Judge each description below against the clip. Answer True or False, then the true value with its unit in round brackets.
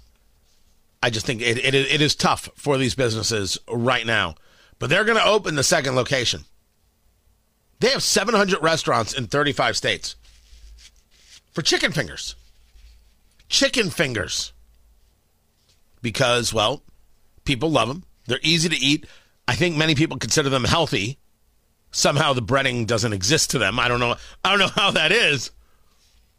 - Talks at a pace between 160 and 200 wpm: False (150 wpm)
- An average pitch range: False (8.6 semitones)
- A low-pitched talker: True (120 Hz)